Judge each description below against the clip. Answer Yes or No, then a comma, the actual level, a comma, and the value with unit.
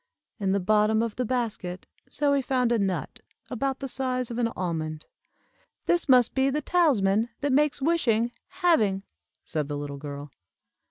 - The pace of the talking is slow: No, average, 160 wpm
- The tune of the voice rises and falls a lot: Yes, wide, 5.9 semitones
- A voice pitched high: Yes, high, 230 Hz